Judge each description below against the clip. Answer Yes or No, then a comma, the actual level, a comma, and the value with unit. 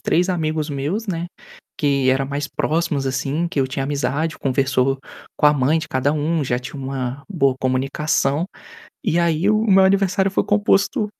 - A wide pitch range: No, average, 4.1 semitones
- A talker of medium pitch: Yes, medium, 150 Hz